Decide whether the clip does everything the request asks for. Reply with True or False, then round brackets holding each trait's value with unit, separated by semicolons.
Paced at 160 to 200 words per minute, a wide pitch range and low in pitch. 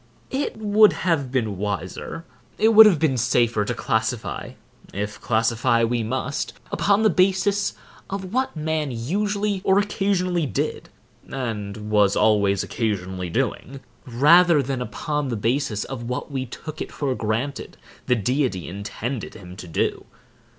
False (145 wpm; 8.4 semitones; 130 Hz)